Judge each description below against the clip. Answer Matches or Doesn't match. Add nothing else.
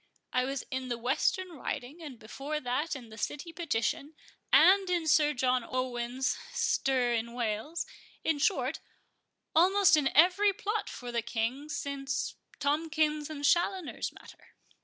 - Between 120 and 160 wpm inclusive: Matches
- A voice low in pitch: Doesn't match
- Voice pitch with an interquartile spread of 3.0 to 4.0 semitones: Doesn't match